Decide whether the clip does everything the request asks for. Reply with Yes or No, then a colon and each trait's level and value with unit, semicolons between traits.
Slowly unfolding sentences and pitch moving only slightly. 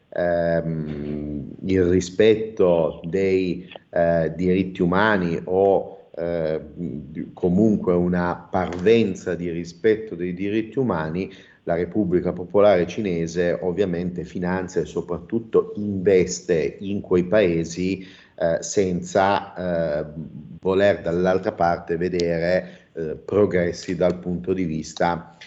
Yes: slow, 100 wpm; narrow, 1.7 semitones